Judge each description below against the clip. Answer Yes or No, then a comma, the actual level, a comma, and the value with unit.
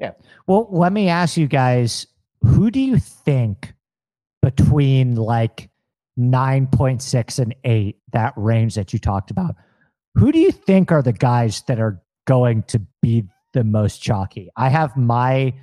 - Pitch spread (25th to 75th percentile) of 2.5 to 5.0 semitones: Yes, average, 3.4 semitones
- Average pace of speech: Yes, average, 155 wpm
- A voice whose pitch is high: No, low, 125 Hz